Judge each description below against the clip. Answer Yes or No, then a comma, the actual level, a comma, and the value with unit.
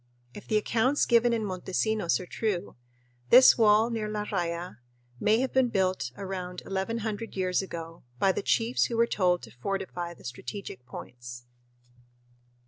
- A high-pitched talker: Yes, high, 195 Hz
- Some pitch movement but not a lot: Yes, average, 4.0 semitones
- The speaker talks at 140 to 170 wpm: Yes, average, 150 wpm